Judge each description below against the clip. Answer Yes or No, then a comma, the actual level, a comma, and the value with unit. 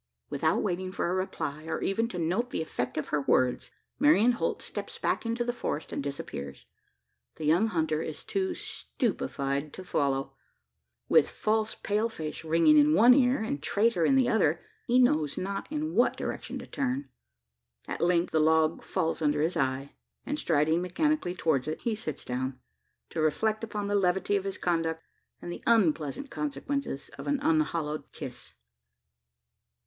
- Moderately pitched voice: Yes, medium, 180 Hz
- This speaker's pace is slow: No, average, 170 wpm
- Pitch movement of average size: No, wide, 7.1 semitones